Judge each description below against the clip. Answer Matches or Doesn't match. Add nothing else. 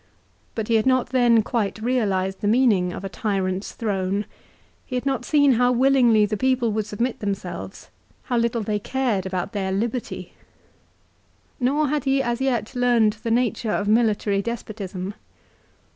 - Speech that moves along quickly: Doesn't match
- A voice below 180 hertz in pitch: Doesn't match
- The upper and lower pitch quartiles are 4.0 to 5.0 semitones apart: Doesn't match